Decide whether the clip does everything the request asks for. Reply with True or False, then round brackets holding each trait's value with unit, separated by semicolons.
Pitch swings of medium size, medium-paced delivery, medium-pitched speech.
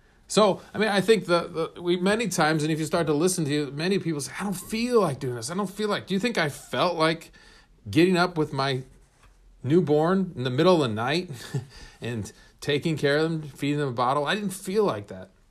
False (4.6 semitones; 240 wpm; 160 Hz)